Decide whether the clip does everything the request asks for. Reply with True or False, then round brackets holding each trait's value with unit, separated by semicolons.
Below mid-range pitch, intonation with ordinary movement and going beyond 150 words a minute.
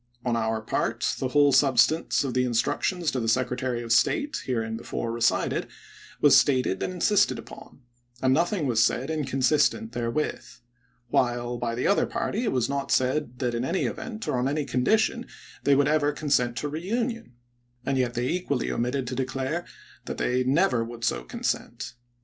True (130 Hz; 3.9 semitones; 175 wpm)